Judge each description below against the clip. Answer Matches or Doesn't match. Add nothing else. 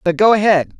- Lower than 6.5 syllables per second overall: Matches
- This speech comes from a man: Doesn't match